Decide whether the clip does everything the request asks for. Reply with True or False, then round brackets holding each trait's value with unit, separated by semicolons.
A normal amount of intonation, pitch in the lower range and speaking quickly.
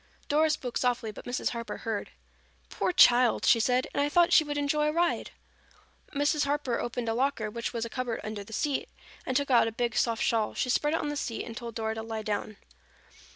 False (4.3 semitones; 245 Hz; 225 wpm)